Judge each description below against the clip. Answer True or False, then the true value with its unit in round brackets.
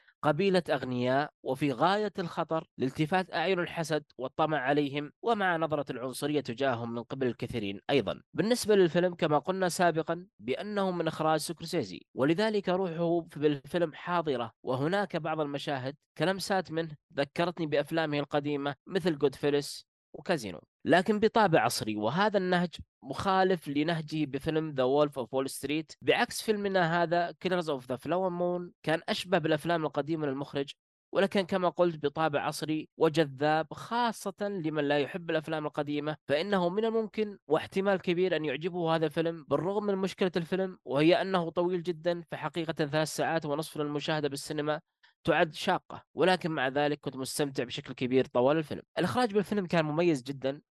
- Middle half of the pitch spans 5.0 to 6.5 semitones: False (3.8 semitones)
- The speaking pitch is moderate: True (160 Hz)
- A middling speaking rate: False (140 wpm)